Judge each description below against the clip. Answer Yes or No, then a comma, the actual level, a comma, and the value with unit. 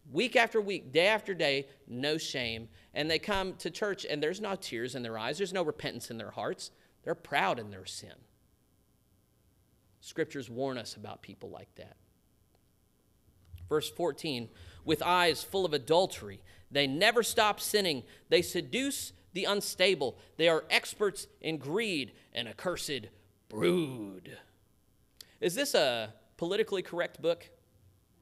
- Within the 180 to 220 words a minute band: No, average, 145 wpm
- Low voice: No, medium, 155 Hz